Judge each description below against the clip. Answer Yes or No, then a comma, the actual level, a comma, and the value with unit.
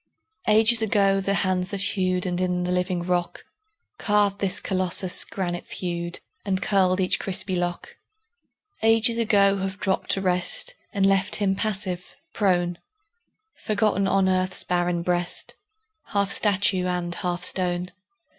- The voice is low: No, medium, 185 Hz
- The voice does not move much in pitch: Yes, narrow, 1.9 semitones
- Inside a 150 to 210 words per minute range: No, slow, 135 wpm